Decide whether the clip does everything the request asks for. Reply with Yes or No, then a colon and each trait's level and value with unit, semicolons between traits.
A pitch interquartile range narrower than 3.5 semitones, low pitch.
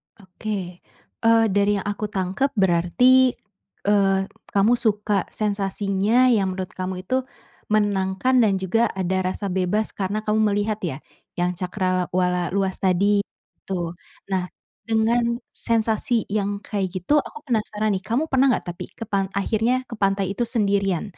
No: average, 2.9 semitones; high, 200 Hz